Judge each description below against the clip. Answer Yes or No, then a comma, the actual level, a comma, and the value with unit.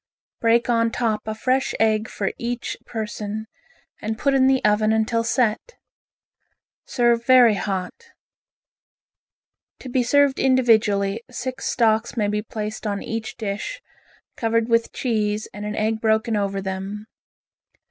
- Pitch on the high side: Yes, high, 225 Hz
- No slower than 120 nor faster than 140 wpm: Yes, slow, 135 wpm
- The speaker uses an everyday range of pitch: No, narrow, 2.3 semitones